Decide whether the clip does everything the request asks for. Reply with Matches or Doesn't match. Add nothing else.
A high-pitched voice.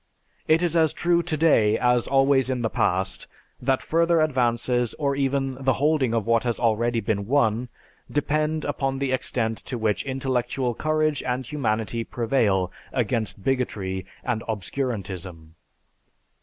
Doesn't match